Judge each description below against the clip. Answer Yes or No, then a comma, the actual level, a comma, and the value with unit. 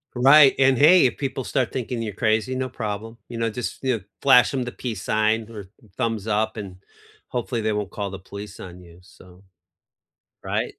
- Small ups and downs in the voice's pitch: No, average, 3.5 semitones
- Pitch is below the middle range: Yes, low, 115 Hz